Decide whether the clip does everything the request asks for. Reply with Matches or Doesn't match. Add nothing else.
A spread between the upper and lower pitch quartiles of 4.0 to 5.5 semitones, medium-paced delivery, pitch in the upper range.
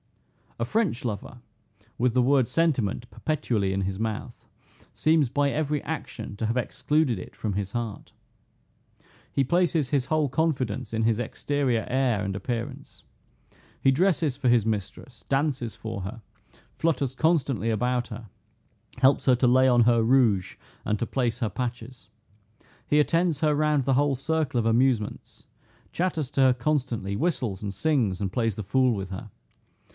Doesn't match